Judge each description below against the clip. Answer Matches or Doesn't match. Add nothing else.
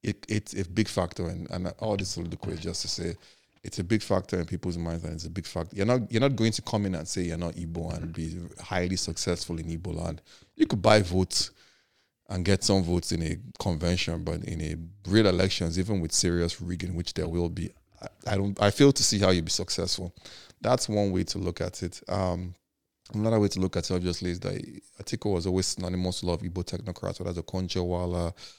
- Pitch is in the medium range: Doesn't match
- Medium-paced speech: Doesn't match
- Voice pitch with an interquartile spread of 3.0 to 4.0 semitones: Doesn't match